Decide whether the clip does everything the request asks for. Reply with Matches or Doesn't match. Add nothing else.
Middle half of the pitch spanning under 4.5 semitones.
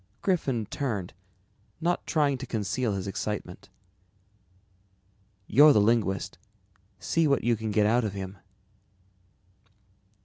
Doesn't match